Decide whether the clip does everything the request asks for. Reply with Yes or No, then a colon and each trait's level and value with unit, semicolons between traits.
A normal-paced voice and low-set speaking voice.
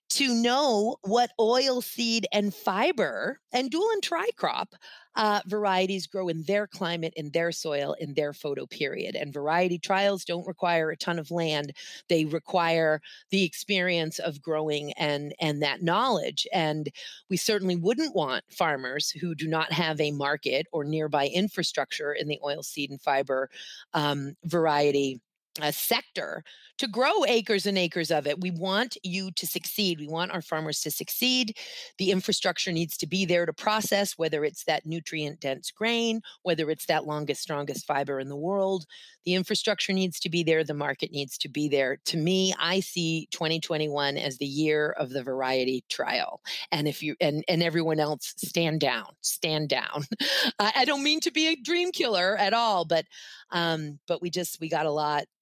No: average, 180 wpm; medium, 170 Hz